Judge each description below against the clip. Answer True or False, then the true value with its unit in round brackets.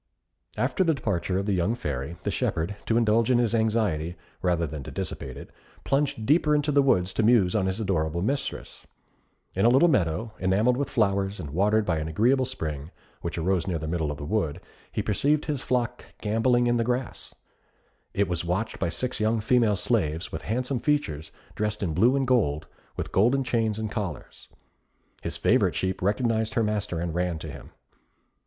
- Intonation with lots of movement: True (5.8 semitones)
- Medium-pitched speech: False (105 Hz)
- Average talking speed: True (190 wpm)